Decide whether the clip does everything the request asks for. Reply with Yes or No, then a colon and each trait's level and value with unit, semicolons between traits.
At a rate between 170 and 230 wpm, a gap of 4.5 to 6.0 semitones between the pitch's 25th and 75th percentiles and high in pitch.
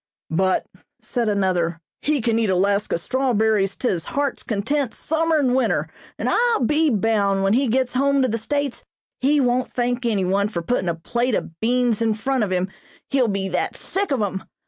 Yes: average, 190 wpm; average, 5.0 semitones; high, 230 Hz